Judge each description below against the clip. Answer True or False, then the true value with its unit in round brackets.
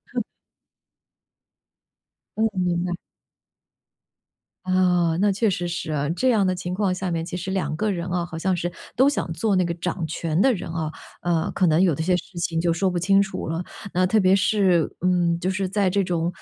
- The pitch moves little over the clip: True (2.1 semitones)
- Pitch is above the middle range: False (180 Hz)